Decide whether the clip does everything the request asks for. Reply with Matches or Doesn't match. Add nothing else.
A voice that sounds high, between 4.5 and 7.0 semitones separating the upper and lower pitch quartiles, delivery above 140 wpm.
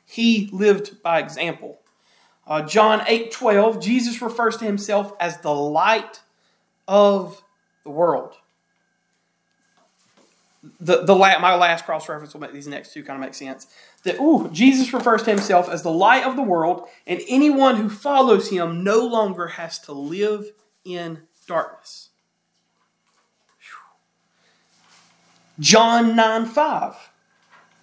Doesn't match